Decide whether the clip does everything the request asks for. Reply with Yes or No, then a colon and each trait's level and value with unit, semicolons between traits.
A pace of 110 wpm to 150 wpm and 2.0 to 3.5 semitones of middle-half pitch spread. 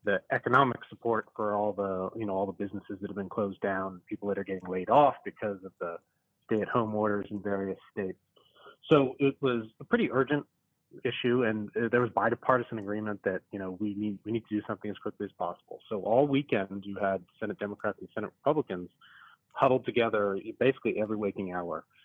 No: average, 200 wpm; narrow, 2.5 semitones